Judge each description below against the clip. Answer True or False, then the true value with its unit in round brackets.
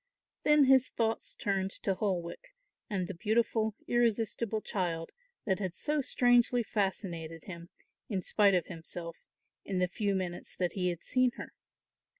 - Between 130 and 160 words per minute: True (150 wpm)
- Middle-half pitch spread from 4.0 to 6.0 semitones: True (4.5 semitones)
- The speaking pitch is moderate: False (200 Hz)